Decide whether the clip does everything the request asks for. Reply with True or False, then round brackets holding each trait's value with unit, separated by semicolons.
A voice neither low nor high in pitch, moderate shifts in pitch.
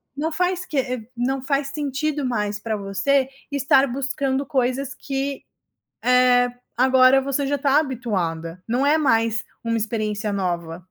False (255 Hz; 3.7 semitones)